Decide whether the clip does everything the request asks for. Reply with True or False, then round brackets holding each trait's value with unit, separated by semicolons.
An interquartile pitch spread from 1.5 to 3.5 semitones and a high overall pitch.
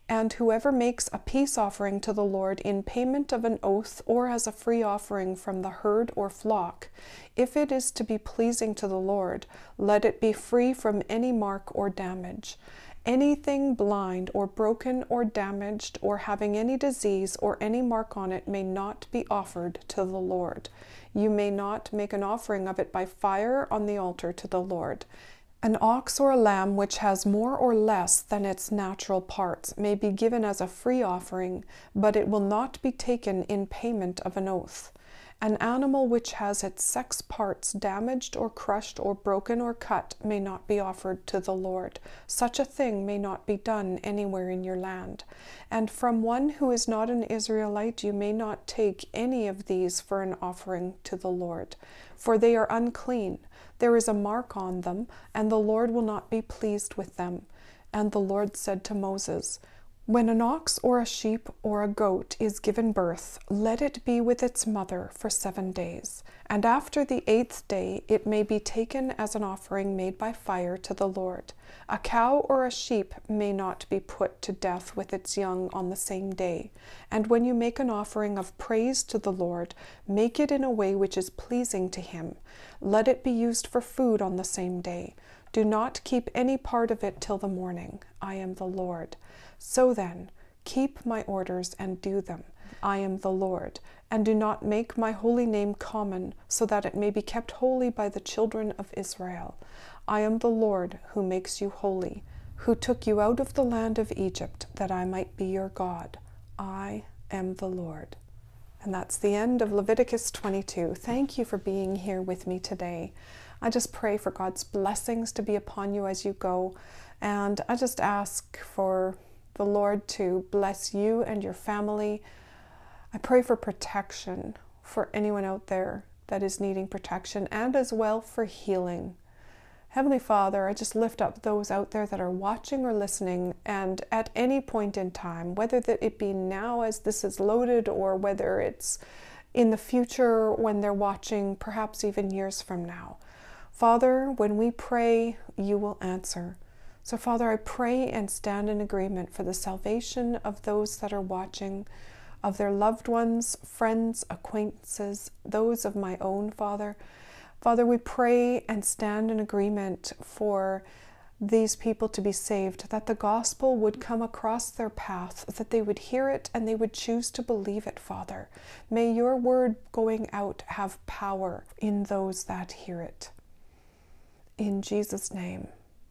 True (3.0 semitones; 210 Hz)